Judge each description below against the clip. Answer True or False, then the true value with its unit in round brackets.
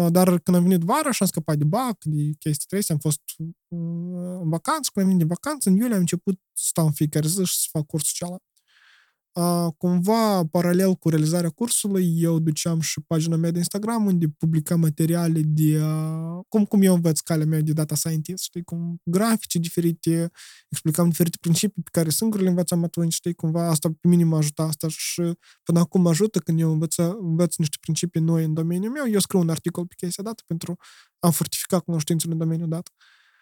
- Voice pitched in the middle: True (170 Hz)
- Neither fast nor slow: False (200 wpm)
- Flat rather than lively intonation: True (2.3 semitones)